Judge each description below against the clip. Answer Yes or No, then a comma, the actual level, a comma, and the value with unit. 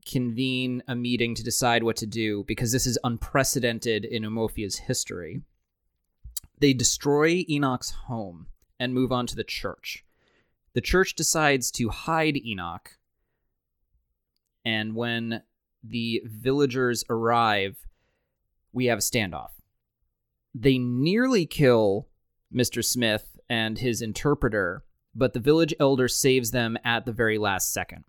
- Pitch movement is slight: No, average, 3.0 semitones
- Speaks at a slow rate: Yes, slow, 125 wpm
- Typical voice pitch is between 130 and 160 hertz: No, low, 120 Hz